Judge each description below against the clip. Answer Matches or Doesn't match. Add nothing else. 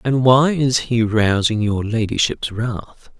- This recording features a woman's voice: Doesn't match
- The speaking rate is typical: Matches